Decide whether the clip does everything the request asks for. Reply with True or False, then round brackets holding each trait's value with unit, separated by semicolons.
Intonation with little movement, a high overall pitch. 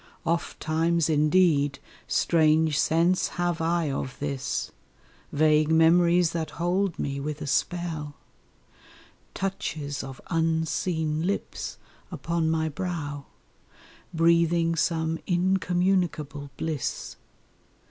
False (2.2 semitones; 160 Hz)